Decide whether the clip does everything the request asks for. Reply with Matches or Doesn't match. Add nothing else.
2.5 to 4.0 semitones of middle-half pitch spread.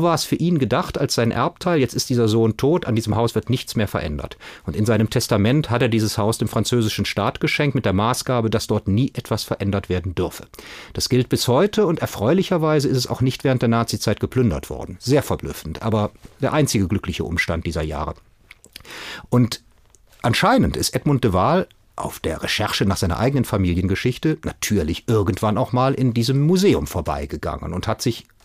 Doesn't match